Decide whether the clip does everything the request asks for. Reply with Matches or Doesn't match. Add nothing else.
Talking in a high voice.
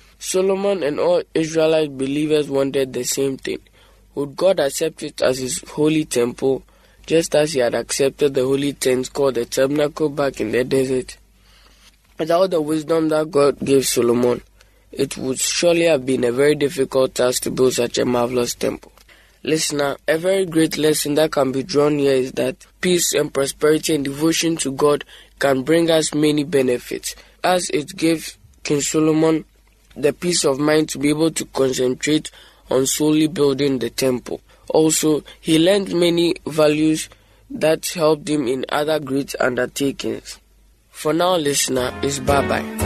Doesn't match